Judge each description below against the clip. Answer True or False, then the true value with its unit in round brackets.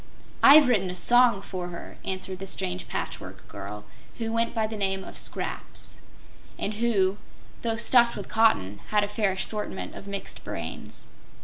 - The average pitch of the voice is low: False (205 Hz)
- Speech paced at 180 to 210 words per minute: False (165 wpm)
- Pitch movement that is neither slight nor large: True (3.4 semitones)